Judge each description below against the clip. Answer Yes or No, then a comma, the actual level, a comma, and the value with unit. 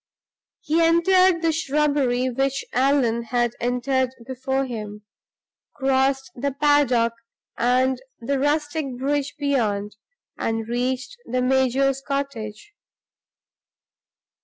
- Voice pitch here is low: No, very high, 265 Hz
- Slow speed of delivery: Yes, slow, 95 wpm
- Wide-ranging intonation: No, average, 2.7 semitones